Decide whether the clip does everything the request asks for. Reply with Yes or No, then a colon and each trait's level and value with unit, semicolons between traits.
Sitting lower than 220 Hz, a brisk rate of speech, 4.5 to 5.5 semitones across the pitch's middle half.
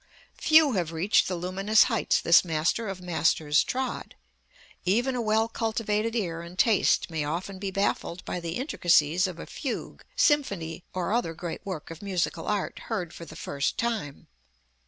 No: medium, 185 Hz; average, 165 wpm; average, 4.8 semitones